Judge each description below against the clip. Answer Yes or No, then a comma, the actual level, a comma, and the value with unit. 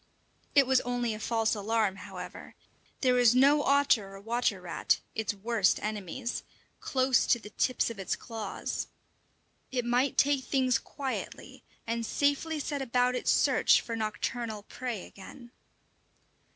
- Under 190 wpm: Yes, average, 140 wpm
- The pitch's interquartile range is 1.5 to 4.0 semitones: Yes, average, 3.2 semitones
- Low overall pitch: No, high, 240 Hz